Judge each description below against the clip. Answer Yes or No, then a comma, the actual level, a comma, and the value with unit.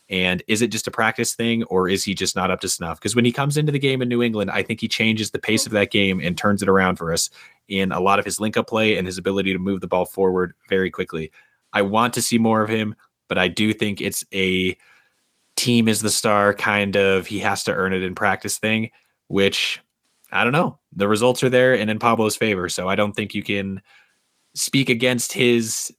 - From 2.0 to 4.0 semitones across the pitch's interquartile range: Yes, average, 2.9 semitones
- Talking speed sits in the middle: No, fast, 245 wpm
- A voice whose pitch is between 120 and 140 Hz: No, low, 105 Hz